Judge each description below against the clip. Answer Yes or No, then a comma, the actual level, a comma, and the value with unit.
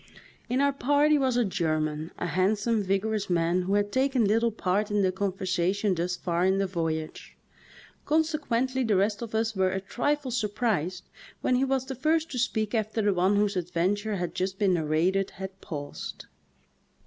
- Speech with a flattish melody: No, average, 4.5 semitones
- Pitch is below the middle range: No, high, 205 Hz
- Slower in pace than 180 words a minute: No, average, 185 wpm